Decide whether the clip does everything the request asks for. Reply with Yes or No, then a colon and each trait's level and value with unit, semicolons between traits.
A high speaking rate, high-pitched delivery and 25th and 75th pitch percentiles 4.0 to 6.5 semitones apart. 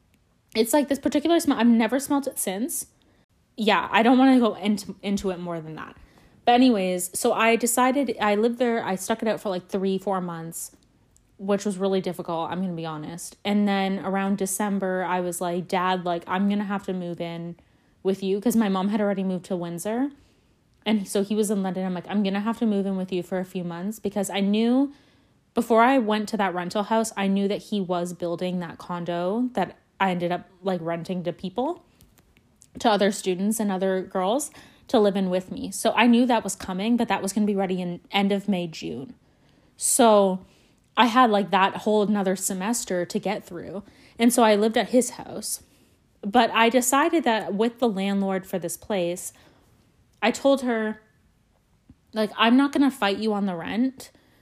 No: fast, 210 wpm; high, 200 Hz; average, 3.4 semitones